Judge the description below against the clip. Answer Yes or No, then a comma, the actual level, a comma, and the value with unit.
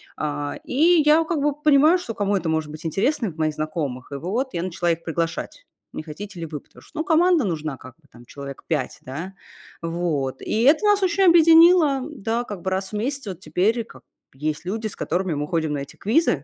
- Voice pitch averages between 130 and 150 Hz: No, high, 190 Hz